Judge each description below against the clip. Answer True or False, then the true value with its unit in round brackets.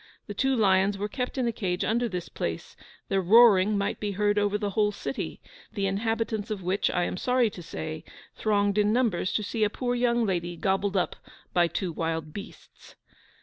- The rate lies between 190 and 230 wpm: True (195 wpm)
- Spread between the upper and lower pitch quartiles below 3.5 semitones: True (3.1 semitones)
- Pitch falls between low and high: False (205 Hz)